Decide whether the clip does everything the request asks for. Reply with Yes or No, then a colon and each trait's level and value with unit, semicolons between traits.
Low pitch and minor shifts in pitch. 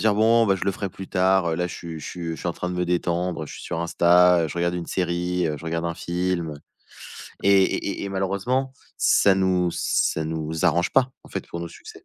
Yes: very low, 90 Hz; narrow, 2.1 semitones